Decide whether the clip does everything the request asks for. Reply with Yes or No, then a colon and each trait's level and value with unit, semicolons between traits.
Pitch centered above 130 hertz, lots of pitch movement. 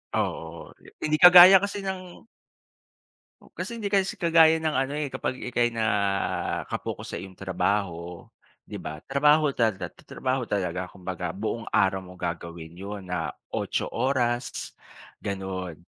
No: low, 110 Hz; wide, 8.5 semitones